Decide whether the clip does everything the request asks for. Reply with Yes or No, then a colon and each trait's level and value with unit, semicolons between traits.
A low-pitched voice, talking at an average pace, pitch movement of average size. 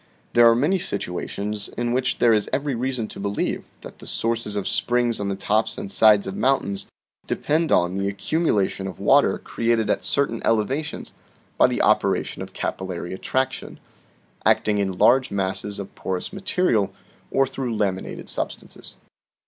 Yes: low, 110 Hz; average, 165 wpm; average, 4.5 semitones